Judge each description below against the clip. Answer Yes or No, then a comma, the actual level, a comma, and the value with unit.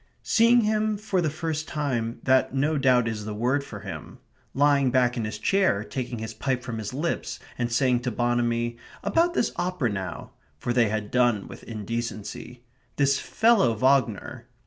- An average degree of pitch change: Yes, average, 4.1 semitones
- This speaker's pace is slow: No, average, 170 wpm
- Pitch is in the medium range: No, low, 125 Hz